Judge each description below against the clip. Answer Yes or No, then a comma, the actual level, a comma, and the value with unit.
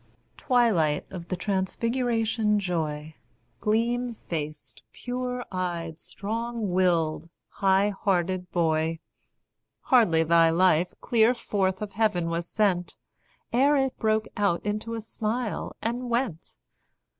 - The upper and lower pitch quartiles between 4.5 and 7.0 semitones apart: Yes, average, 5.1 semitones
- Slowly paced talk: Yes, slow, 110 wpm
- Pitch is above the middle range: Yes, high, 200 Hz